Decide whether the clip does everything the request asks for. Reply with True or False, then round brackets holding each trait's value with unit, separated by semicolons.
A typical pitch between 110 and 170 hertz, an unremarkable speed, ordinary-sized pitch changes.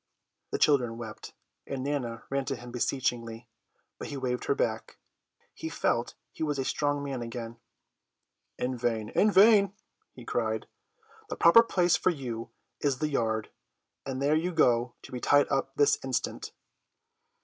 True (135 Hz; 160 wpm; 3.6 semitones)